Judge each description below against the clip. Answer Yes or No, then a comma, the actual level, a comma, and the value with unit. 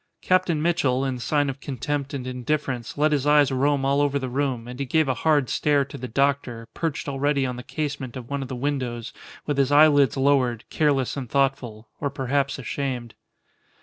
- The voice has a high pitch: No, medium, 140 Hz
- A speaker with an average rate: Yes, average, 195 wpm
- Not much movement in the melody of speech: Yes, narrow, 2.2 semitones